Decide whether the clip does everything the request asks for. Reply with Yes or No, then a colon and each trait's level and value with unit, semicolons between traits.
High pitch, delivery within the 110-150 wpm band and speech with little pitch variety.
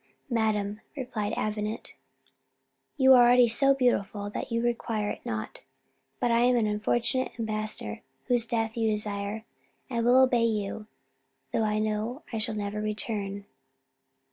Yes: high, 220 Hz; average, 140 wpm; narrow, 2.3 semitones